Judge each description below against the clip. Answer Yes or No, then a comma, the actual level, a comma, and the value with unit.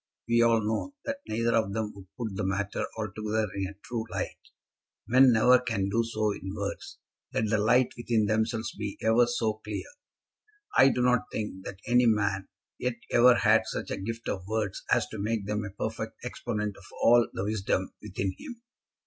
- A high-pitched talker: No, low, 110 Hz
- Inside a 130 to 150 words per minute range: No, average, 190 wpm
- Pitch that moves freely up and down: No, narrow, 2.5 semitones